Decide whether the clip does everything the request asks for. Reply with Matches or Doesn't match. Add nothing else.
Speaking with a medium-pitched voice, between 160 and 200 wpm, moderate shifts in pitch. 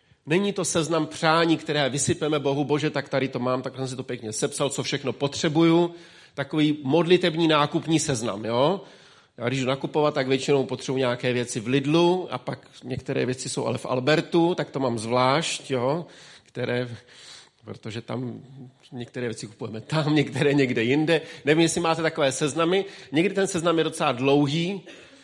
Matches